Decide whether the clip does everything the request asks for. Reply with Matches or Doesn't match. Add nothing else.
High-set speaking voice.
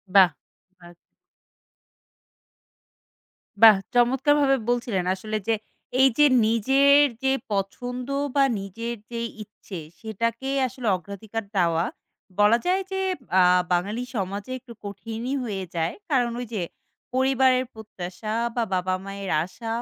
Matches